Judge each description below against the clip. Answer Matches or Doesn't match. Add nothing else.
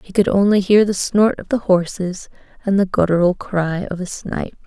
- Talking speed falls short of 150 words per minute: Doesn't match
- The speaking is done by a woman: Matches